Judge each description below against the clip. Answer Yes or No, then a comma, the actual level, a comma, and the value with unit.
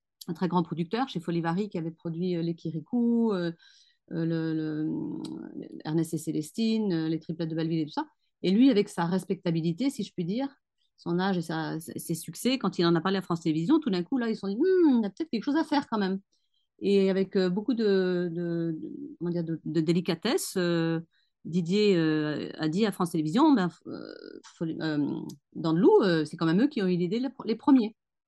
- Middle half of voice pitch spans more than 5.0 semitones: Yes, wide, 5.6 semitones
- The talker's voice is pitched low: No, medium, 180 Hz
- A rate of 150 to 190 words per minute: No, average, 215 wpm